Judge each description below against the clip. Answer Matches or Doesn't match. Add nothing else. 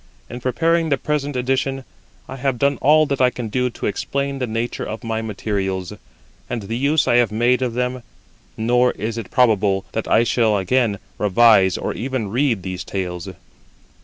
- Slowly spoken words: Doesn't match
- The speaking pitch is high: Doesn't match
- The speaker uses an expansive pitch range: Doesn't match